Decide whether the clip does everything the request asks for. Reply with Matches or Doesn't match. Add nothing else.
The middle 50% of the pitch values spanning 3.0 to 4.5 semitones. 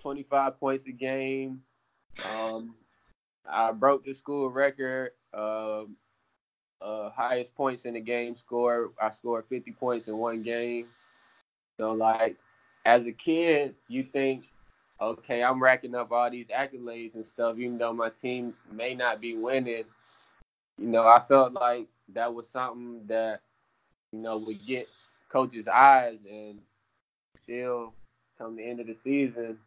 Doesn't match